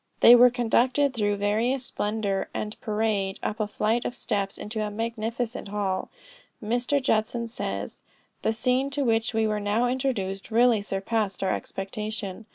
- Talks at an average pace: Yes, average, 155 wpm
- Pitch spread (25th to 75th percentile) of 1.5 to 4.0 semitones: Yes, average, 2.7 semitones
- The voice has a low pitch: No, high, 220 Hz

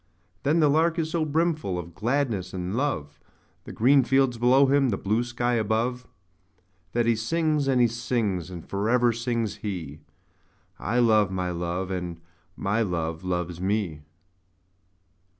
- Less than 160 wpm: Yes, average, 150 wpm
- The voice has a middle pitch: No, low, 115 Hz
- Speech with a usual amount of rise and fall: No, wide, 6.1 semitones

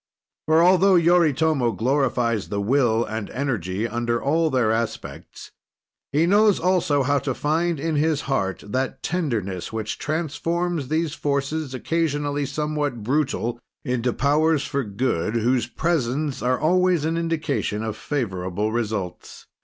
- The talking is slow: Yes, slow, 130 wpm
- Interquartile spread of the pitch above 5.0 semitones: Yes, wide, 5.4 semitones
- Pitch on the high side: No, medium, 140 Hz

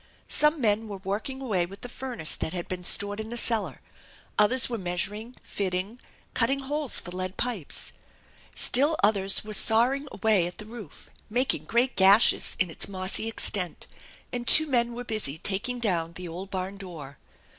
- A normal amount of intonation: Yes, average, 4.5 semitones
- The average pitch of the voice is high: Yes, high, 210 Hz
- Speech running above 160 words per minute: Yes, average, 170 wpm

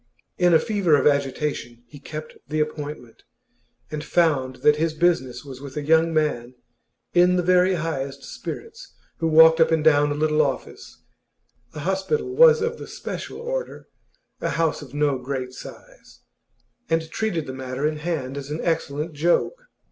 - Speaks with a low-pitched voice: No, medium, 155 Hz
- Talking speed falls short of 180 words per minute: Yes, average, 165 wpm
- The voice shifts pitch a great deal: No, average, 3.2 semitones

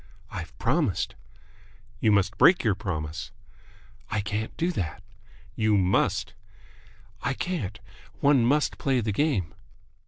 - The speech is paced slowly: Yes, slow, 120 wpm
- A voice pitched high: No, low, 105 Hz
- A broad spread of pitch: Yes, wide, 6.5 semitones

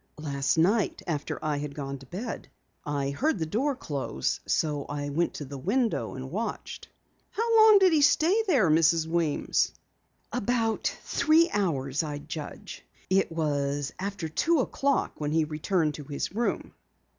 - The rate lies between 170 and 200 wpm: No, average, 155 wpm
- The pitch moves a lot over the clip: Yes, wide, 8.1 semitones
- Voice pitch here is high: No, medium, 160 Hz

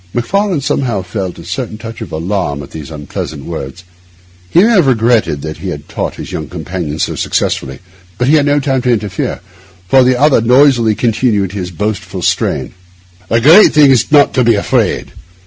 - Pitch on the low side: Yes, low, 110 Hz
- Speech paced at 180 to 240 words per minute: Yes, average, 190 wpm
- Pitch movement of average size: No, wide, 7.0 semitones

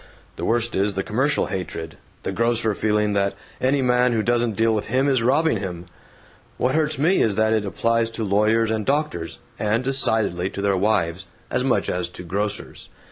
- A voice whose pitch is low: Yes, low, 110 Hz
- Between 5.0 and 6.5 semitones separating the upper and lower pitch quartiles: No, average, 3.8 semitones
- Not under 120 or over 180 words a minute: No, average, 190 wpm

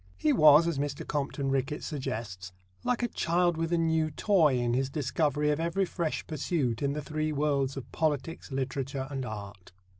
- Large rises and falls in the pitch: No, average, 3.2 semitones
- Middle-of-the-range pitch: Yes, medium, 145 Hz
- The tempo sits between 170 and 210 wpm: Yes, average, 180 wpm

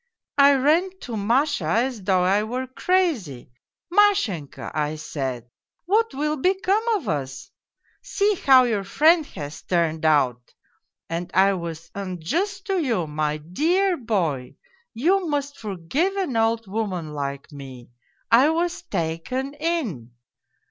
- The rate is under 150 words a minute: Yes, average, 140 wpm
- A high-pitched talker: Yes, high, 225 Hz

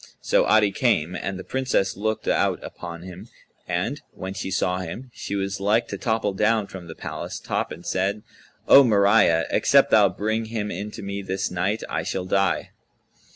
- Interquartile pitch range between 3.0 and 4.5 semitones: No, narrow, 2.6 semitones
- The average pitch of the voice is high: No, low, 100 Hz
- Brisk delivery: No, average, 185 wpm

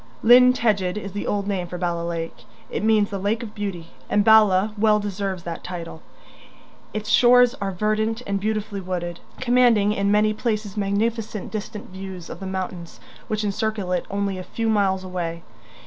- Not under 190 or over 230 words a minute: No, average, 175 wpm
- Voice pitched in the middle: No, high, 200 Hz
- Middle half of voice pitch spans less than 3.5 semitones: Yes, average, 2.7 semitones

